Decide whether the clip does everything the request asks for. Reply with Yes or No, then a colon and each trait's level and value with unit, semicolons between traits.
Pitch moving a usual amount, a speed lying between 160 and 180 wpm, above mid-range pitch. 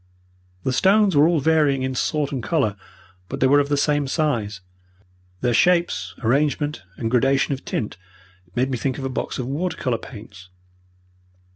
No: average, 3.4 semitones; average, 170 wpm; low, 135 Hz